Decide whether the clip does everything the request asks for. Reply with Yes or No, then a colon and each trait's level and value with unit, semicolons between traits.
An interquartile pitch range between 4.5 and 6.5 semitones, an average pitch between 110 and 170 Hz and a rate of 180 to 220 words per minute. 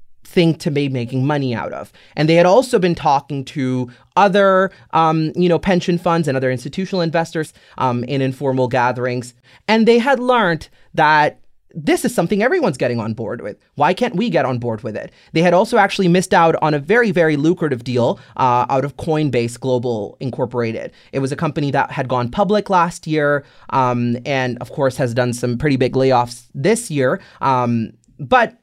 Yes: wide, 5.5 semitones; medium, 140 Hz; average, 190 wpm